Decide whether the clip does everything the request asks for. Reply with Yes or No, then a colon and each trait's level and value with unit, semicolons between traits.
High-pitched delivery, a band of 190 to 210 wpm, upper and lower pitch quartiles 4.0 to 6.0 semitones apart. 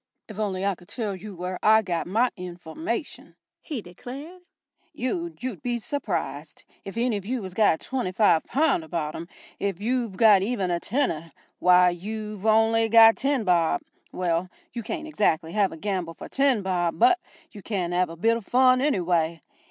No: high, 205 Hz; average, 180 wpm; wide, 5.5 semitones